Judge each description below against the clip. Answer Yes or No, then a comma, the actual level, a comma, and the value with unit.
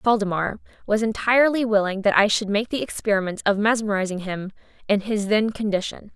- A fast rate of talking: No, average, 165 wpm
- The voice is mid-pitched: No, high, 210 Hz